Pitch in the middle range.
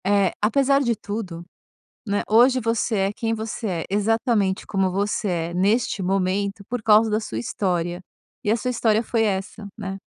No: high, 210 Hz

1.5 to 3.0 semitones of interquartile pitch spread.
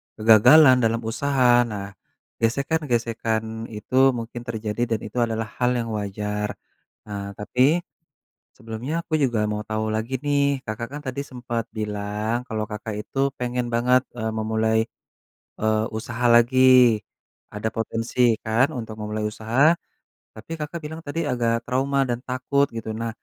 Yes: average, 2.7 semitones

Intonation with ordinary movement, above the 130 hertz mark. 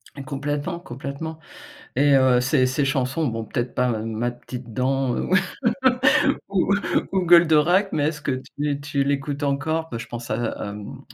Yes: average, 3.1 semitones; medium, 140 Hz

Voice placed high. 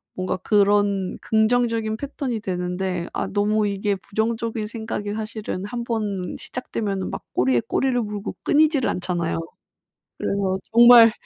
Yes: high, 210 Hz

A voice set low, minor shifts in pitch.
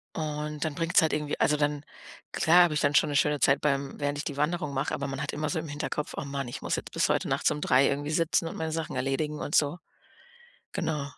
No: medium, 150 Hz; narrow, 1.6 semitones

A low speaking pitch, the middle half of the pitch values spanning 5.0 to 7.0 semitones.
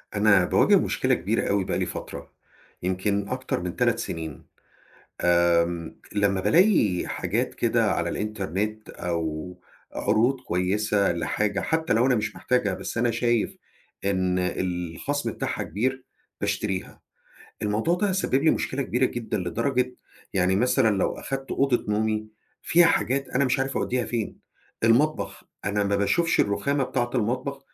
Yes: low, 110 Hz; wide, 5.5 semitones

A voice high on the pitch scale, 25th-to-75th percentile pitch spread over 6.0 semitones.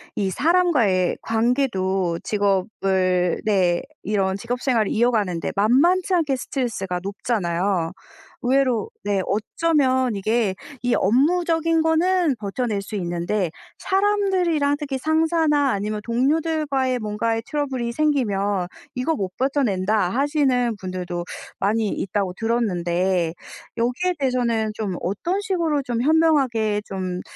Yes: high, 230 Hz; wide, 6.7 semitones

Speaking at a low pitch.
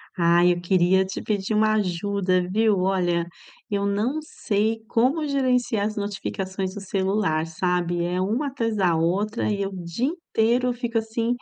No: high, 200 Hz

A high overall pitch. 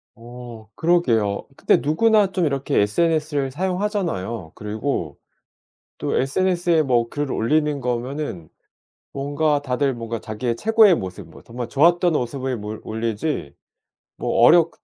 No: low, 135 Hz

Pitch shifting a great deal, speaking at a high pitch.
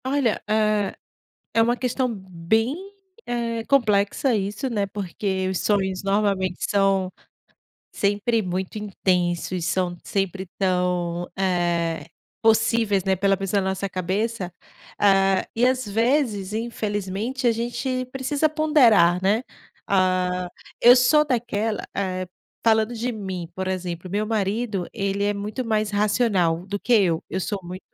No: average, 3.5 semitones; high, 200 Hz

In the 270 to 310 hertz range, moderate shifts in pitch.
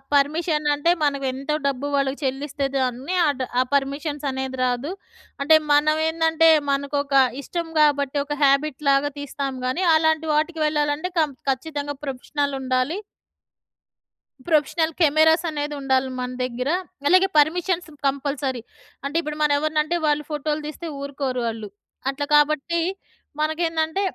No: very high, 290 Hz; narrow, 2.3 semitones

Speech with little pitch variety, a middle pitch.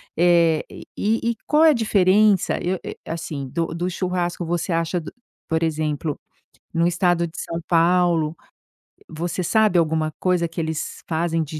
Yes: narrow, 2.1 semitones; medium, 170 Hz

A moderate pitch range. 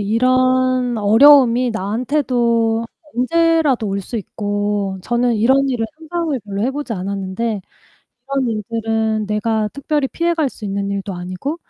Yes: average, 4.2 semitones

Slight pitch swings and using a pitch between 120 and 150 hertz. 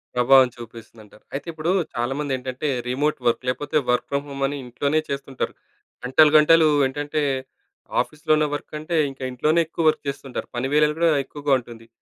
No: average, 3.2 semitones; medium, 140 Hz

